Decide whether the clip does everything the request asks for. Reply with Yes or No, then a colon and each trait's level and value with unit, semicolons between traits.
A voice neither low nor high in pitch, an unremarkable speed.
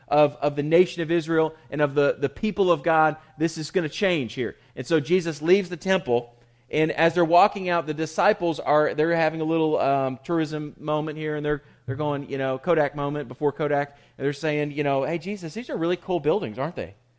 No: medium, 155 Hz; fast, 225 wpm